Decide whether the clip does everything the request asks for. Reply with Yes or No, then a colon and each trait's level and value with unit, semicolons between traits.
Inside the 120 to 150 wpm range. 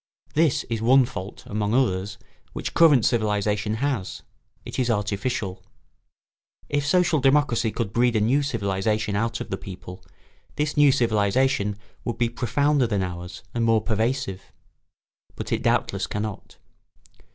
Yes: average, 140 wpm